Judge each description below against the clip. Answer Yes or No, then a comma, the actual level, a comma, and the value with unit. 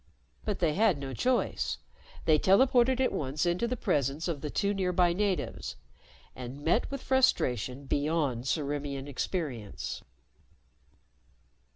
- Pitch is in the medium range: Yes, medium, 160 Hz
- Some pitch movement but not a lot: No, wide, 6.5 semitones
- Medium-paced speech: No, slow, 125 wpm